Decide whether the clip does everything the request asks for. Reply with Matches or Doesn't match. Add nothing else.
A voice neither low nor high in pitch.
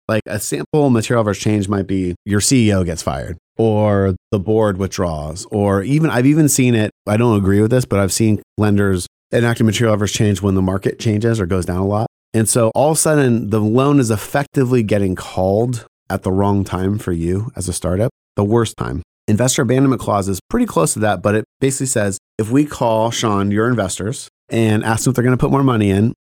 Doesn't match